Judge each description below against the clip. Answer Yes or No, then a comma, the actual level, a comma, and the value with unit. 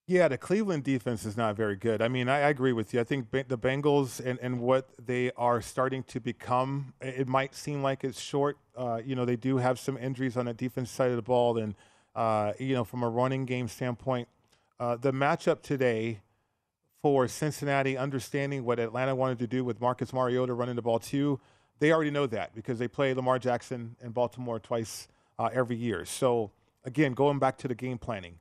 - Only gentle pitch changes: Yes, narrow, 2.1 semitones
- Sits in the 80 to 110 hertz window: No, low, 125 Hz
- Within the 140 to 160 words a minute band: No, fast, 205 wpm